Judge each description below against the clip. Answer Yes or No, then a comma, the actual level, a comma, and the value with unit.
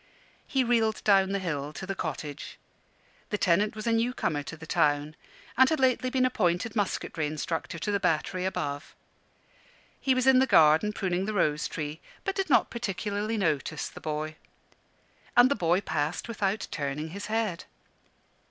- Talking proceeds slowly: No, average, 165 wpm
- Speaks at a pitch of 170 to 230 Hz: Yes, high, 190 Hz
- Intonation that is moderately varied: No, wide, 6.4 semitones